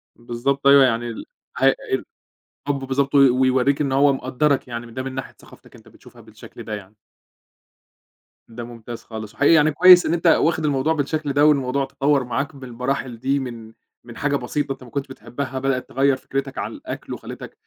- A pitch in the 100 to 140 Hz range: Yes, low, 135 Hz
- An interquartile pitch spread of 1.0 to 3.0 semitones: Yes, narrow, 2.5 semitones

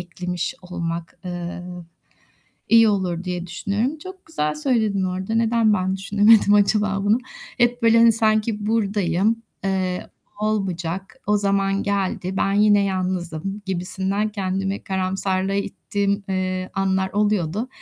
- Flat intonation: Yes, narrow, 2.3 semitones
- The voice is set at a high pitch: Yes, high, 195 Hz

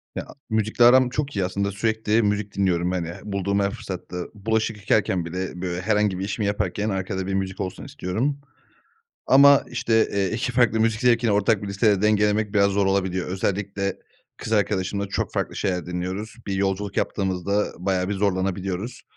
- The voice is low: Yes, low, 100 Hz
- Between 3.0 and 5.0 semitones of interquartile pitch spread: No, narrow, 2.6 semitones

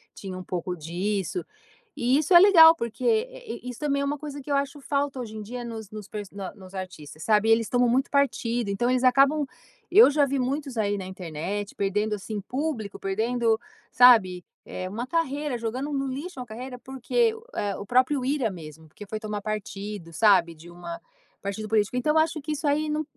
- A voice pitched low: No, high, 235 Hz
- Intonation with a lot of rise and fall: Yes, wide, 5.7 semitones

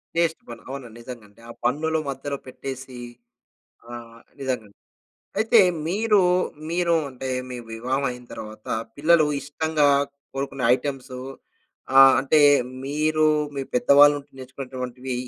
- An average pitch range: Yes, average, 3.3 semitones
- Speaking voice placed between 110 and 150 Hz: Yes, low, 135 Hz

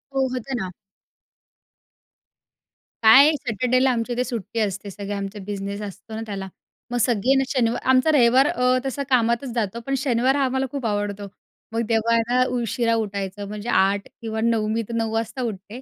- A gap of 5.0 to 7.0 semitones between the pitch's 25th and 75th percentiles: No, average, 3.6 semitones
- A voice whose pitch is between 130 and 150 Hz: No, high, 230 Hz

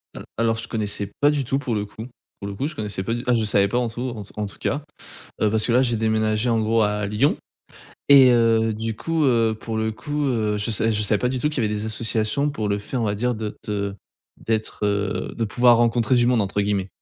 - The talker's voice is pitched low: Yes, low, 110 Hz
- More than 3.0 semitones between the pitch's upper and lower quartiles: No, average, 2.7 semitones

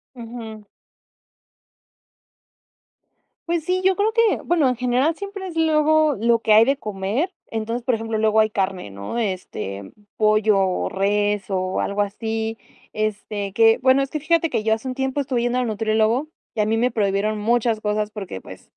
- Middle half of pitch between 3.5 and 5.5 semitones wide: Yes, average, 4.2 semitones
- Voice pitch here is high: Yes, high, 225 Hz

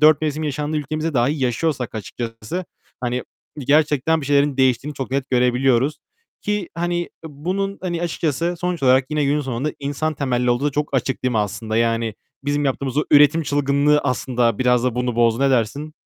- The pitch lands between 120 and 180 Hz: Yes, medium, 140 Hz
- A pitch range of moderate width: Yes, average, 3.5 semitones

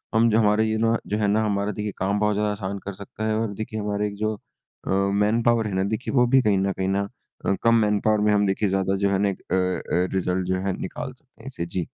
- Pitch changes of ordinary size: No, narrow, 1.9 semitones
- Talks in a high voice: No, low, 105 Hz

